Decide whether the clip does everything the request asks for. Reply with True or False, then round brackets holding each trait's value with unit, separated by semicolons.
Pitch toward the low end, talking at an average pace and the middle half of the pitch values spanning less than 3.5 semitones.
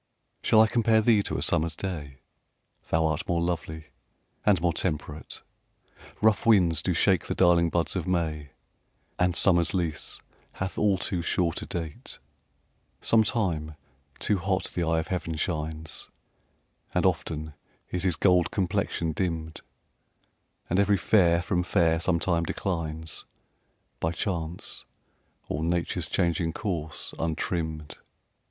False (85 Hz; 130 wpm; 2.6 semitones)